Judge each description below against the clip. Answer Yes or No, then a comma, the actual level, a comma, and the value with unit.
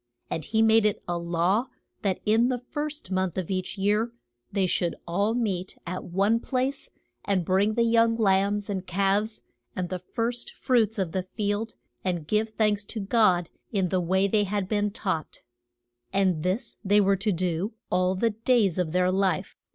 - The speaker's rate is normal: Yes, average, 180 wpm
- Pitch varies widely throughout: No, average, 3.2 semitones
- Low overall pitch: No, high, 200 Hz